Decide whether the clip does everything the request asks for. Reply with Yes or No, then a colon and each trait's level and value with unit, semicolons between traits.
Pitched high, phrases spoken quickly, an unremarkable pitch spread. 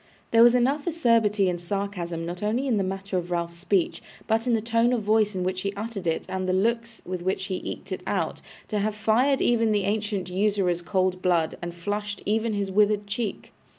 Yes: high, 205 Hz; fast, 215 wpm; average, 3.2 semitones